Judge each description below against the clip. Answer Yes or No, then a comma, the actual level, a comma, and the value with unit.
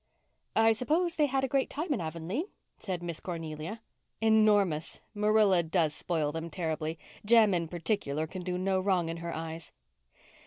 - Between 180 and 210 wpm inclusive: No, average, 160 wpm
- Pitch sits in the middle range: Yes, medium, 180 Hz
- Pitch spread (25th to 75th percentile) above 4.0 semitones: Yes, average, 5.0 semitones